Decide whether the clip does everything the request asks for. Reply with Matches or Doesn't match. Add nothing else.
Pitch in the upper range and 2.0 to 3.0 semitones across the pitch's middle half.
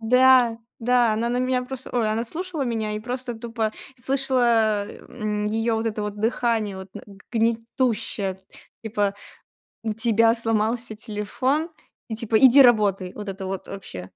Matches